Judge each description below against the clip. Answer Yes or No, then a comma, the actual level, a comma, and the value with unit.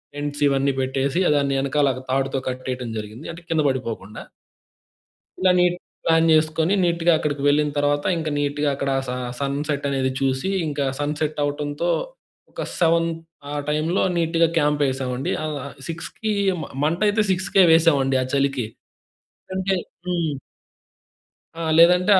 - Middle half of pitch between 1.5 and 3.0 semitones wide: No, average, 3.4 semitones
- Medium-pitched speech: Yes, medium, 145 Hz